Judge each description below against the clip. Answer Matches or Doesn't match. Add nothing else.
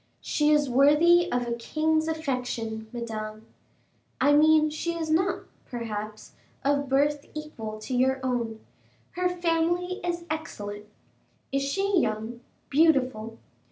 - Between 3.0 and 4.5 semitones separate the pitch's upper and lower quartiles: Doesn't match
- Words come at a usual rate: Doesn't match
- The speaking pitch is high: Matches